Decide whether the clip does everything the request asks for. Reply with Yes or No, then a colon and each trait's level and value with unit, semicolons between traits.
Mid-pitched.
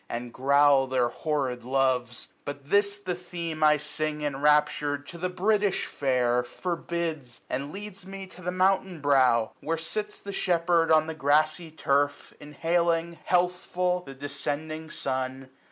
Yes: medium, 155 Hz